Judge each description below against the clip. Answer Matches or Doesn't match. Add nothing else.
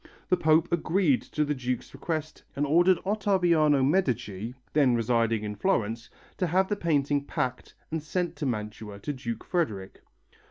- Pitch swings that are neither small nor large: Doesn't match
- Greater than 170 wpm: Doesn't match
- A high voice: Doesn't match